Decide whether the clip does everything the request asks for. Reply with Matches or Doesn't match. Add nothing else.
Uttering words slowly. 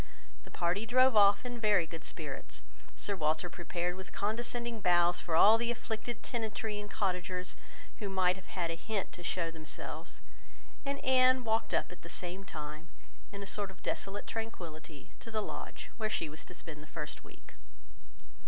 Doesn't match